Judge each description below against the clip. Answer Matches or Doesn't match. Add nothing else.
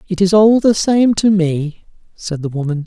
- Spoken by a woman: Doesn't match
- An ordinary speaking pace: Doesn't match